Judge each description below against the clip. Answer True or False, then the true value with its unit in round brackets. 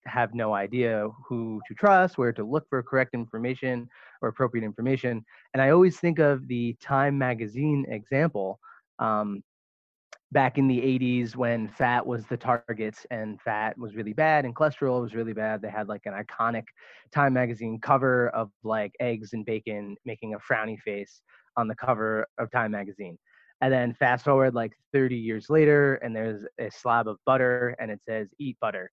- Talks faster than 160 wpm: True (180 wpm)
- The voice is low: True (120 Hz)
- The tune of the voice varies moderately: True (3.1 semitones)